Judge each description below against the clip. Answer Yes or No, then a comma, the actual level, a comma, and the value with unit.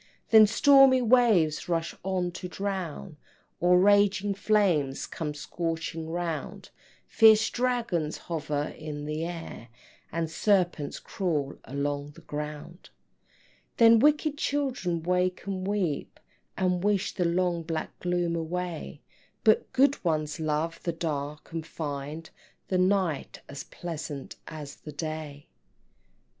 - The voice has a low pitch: No, medium, 170 Hz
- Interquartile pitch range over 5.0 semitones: No, average, 4.3 semitones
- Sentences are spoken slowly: Yes, slow, 120 wpm